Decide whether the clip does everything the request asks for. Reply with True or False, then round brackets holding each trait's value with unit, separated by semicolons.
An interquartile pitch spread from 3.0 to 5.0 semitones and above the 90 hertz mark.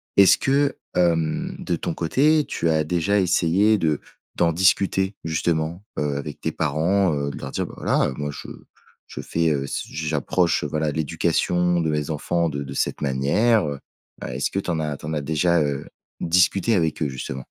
False (3.3 semitones; 80 Hz)